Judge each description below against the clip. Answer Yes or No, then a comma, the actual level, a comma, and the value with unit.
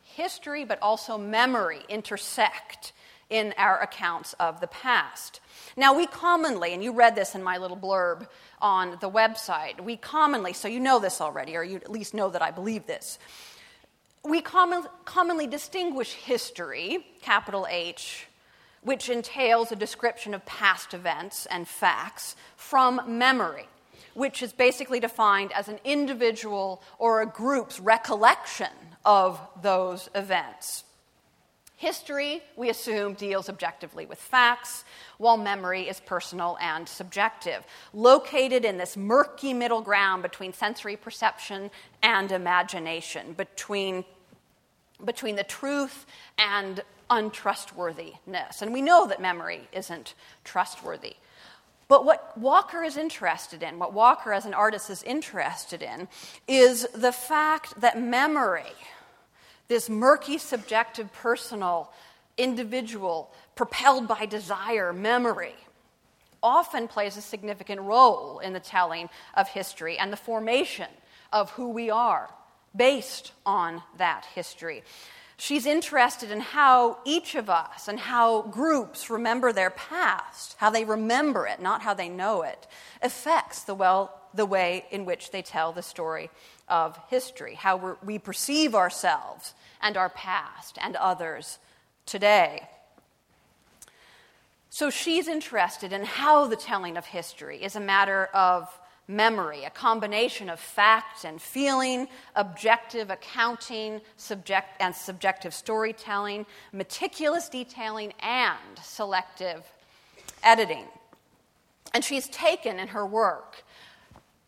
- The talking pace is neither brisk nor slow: No, slow, 125 wpm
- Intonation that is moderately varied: Yes, average, 5.0 semitones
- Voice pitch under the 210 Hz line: No, high, 220 Hz